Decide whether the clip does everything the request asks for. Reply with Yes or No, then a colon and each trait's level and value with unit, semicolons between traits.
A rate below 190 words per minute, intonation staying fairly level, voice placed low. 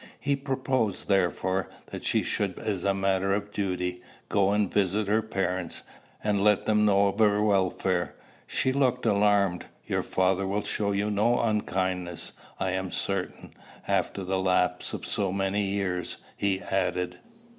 Yes: average, 155 wpm; narrow, 1.9 semitones; low, 100 Hz